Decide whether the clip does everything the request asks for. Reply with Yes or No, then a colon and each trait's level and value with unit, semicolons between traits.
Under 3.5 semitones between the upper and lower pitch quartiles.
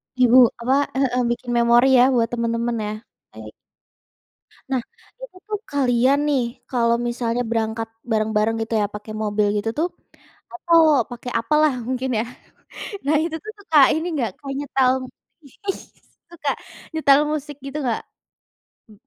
No: average, 3.8 semitones